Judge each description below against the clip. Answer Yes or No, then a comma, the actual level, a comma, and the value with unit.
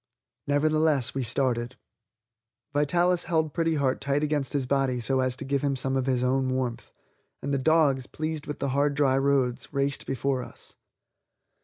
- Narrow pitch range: Yes, narrow, 2.1 semitones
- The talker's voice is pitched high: No, medium, 140 Hz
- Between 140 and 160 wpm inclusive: No, average, 170 wpm